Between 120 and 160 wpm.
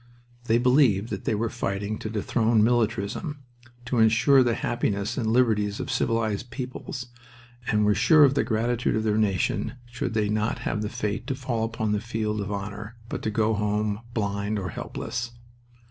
No: average, 175 wpm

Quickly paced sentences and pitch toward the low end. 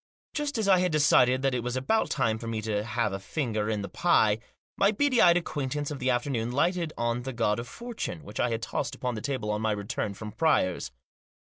Yes: fast, 235 wpm; low, 125 Hz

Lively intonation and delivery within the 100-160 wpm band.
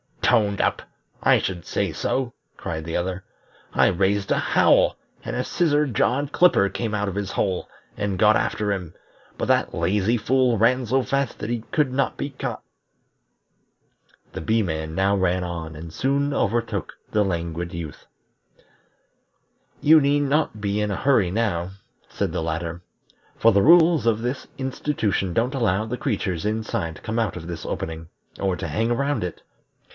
No: wide, 6.0 semitones; average, 170 wpm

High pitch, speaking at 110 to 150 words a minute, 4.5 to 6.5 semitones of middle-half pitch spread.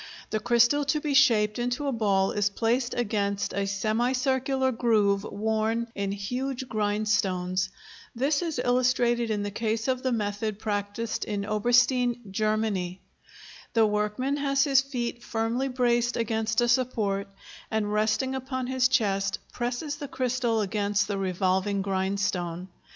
No: high, 225 Hz; average, 140 wpm; average, 3.7 semitones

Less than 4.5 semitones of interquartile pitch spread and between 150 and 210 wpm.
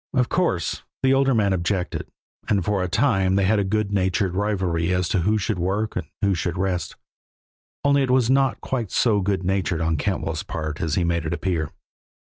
Yes: average, 3.6 semitones; average, 200 wpm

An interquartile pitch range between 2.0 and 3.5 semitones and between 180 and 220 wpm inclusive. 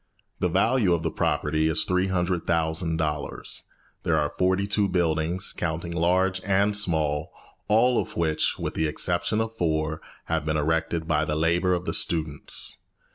No: average, 2.9 semitones; average, 150 wpm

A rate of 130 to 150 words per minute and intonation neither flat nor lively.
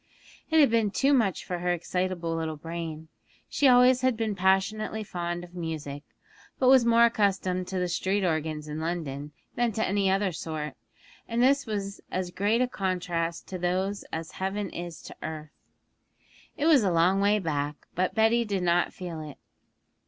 No: average, 175 wpm; average, 4.4 semitones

